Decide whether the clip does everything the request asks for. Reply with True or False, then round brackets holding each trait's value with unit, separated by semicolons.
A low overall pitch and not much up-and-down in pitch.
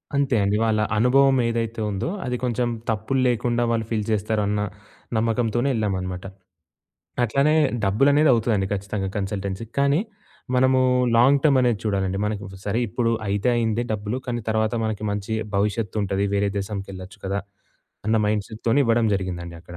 False (110 Hz; 3.1 semitones)